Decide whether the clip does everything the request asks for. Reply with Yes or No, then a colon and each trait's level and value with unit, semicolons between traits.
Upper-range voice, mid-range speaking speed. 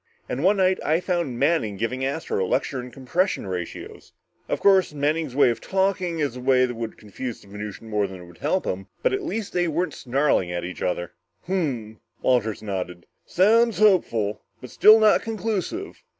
No: low, 135 Hz; average, 190 wpm